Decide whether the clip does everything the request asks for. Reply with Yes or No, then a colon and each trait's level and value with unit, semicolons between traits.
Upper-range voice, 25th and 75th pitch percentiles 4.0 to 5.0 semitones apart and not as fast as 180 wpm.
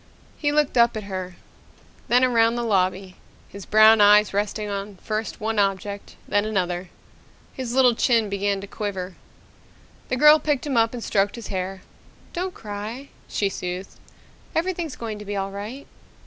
No: high, 210 Hz; average, 3.3 semitones; average, 160 wpm